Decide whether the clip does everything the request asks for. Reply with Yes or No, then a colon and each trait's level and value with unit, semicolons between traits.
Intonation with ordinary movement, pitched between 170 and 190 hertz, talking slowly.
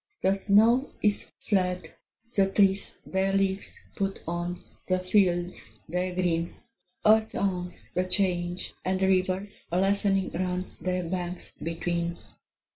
No: narrow, 1.7 semitones; medium, 185 Hz; slow, 120 wpm